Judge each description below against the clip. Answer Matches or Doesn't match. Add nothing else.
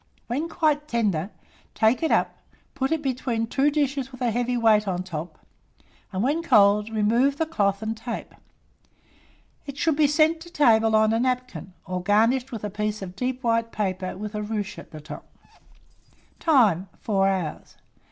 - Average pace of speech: Matches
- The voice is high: Matches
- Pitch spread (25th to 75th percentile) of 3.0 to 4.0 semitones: Doesn't match